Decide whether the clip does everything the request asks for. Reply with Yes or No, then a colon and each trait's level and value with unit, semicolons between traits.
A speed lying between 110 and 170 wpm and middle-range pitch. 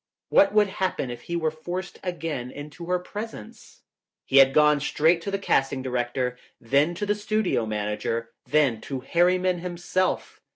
Yes: average, 160 wpm; medium, 160 Hz